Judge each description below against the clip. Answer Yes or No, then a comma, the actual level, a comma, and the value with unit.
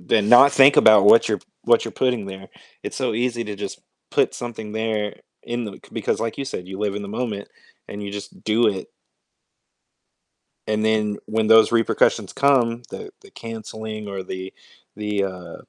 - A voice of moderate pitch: No, low, 110 Hz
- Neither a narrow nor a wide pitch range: No, narrow, 2.3 semitones